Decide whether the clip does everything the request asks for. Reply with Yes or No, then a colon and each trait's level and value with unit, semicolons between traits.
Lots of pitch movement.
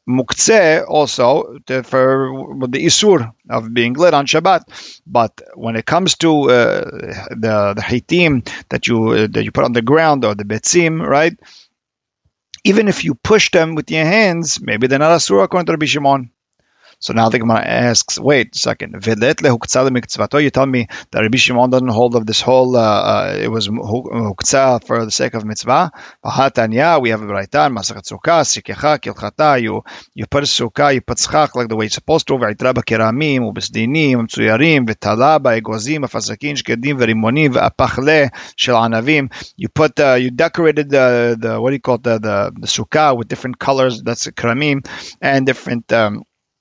No: average, 4.3 semitones